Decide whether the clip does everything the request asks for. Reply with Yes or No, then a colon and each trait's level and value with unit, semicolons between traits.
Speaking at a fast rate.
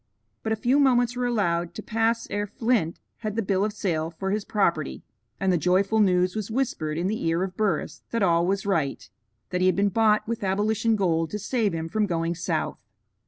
Yes: fast, 215 wpm